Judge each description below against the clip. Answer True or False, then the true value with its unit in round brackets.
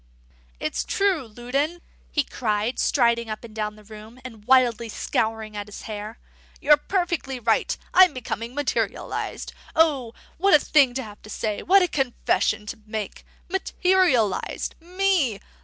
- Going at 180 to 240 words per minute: False (145 wpm)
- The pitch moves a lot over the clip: True (6.0 semitones)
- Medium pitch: False (245 Hz)